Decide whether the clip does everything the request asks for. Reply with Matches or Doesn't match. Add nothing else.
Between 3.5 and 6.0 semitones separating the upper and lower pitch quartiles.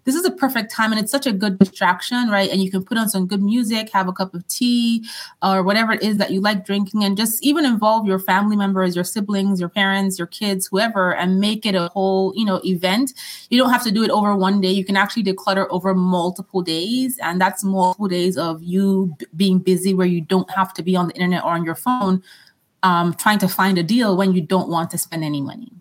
Doesn't match